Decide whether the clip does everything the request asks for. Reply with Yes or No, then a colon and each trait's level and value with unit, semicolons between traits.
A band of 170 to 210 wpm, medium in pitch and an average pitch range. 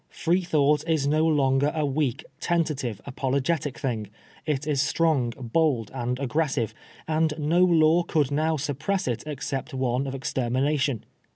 No: slow, 135 wpm; medium, 145 Hz; average, 3.1 semitones